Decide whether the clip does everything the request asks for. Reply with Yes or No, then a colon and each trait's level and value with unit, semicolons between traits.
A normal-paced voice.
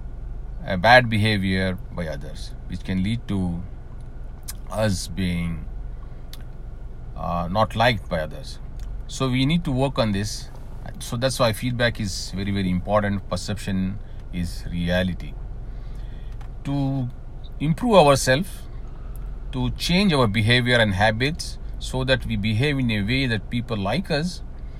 No: slow, 130 wpm